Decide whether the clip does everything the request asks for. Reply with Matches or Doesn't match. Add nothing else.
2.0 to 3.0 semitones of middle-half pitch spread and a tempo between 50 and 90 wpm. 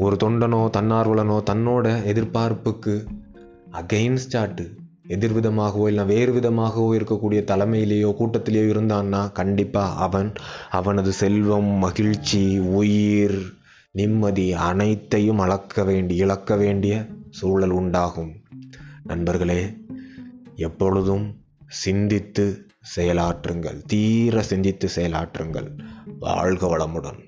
Matches